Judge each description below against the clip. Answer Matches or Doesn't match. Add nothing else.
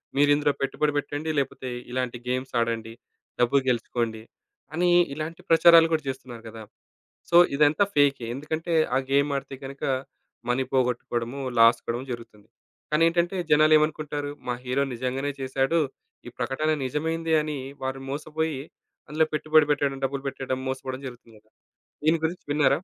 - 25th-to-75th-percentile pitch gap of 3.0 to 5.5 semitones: Matches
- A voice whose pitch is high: Doesn't match